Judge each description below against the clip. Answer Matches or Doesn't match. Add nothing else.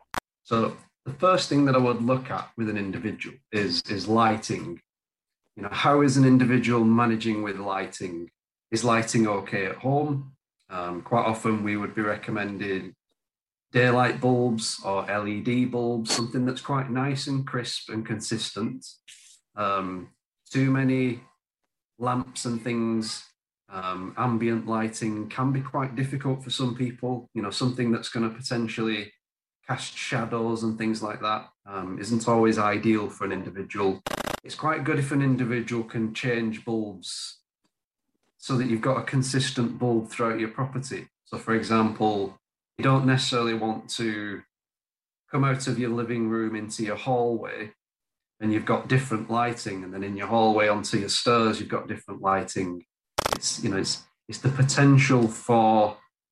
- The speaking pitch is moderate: Doesn't match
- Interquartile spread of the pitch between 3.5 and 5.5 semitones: Doesn't match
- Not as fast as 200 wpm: Matches